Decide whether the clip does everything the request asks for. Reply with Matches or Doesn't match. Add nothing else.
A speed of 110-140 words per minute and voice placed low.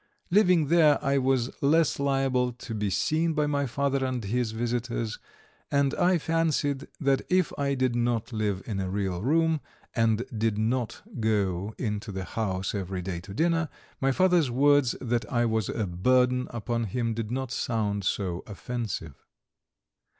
Doesn't match